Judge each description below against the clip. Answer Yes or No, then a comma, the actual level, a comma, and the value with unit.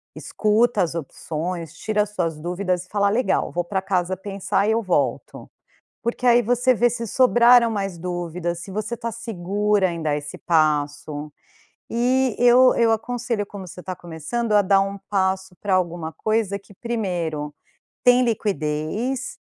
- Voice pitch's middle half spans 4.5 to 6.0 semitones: Yes, average, 5.0 semitones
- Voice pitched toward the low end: No, high, 195 Hz